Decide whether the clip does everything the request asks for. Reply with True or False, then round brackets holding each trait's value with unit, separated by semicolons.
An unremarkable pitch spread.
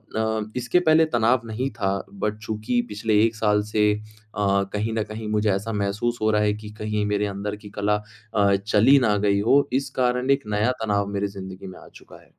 False (1.7 semitones)